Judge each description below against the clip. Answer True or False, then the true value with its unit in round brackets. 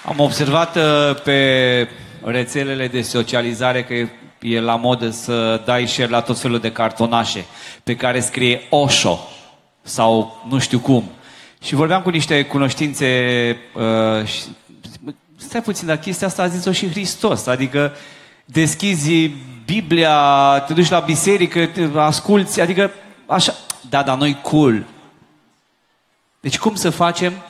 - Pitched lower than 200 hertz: True (140 Hz)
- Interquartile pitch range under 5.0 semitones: False (5.6 semitones)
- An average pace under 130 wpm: False (140 wpm)